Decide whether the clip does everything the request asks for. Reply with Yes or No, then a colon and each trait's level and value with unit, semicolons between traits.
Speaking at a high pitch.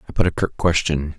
No: very low, 80 Hz